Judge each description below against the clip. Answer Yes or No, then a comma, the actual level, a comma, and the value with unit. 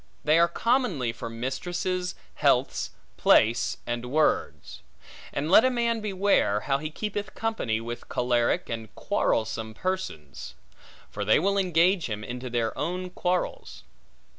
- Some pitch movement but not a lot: No, wide, 8.2 semitones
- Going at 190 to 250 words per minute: No, slow, 135 wpm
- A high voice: No, medium, 155 Hz